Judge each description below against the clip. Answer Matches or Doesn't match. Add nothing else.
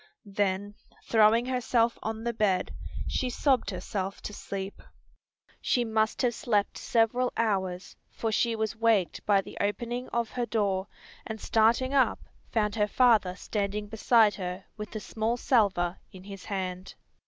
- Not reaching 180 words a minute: Matches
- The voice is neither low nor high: Doesn't match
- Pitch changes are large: Doesn't match